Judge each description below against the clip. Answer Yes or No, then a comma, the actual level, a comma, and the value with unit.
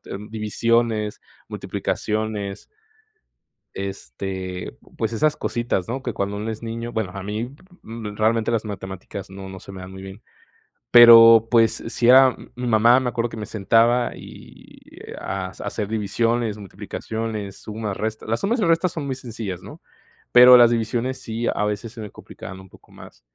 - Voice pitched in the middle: No, low, 110 Hz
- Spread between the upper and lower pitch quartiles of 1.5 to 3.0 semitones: Yes, average, 2.7 semitones